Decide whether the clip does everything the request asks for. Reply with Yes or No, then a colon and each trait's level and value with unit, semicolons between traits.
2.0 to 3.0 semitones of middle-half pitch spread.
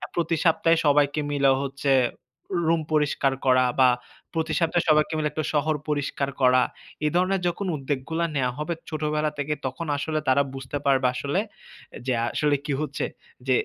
Yes: narrow, 2.5 semitones